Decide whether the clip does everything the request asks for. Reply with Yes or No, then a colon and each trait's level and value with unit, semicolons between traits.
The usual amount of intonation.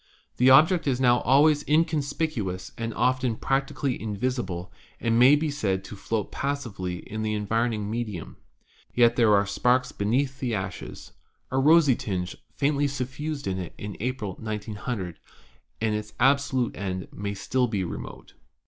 Yes: average, 4.8 semitones